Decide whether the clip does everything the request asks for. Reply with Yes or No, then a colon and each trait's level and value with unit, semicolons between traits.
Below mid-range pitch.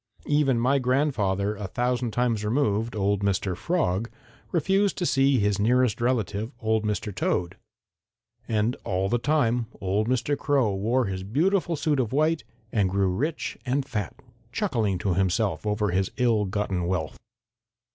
Yes: low, 110 Hz